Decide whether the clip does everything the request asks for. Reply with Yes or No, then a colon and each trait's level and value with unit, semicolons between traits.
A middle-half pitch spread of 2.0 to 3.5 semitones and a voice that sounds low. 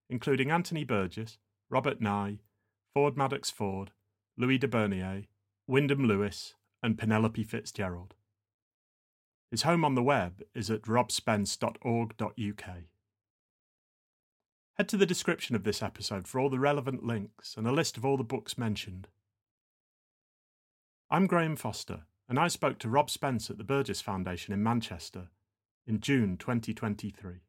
No: average, 4.0 semitones; low, 110 Hz